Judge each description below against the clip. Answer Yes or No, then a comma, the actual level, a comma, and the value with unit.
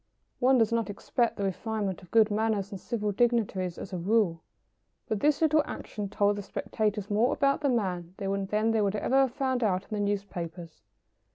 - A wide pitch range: No, average, 3.0 semitones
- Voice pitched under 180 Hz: No, high, 210 Hz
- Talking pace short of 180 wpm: No, average, 190 wpm